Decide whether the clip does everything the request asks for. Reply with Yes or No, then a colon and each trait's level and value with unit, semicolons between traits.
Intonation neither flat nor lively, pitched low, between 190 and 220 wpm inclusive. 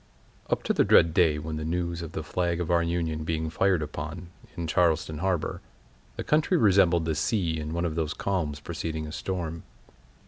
No: narrow, 1.9 semitones; very low, 85 Hz; average, 195 wpm